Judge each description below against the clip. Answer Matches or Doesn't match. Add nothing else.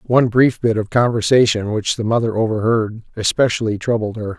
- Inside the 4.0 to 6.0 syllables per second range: Matches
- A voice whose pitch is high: Doesn't match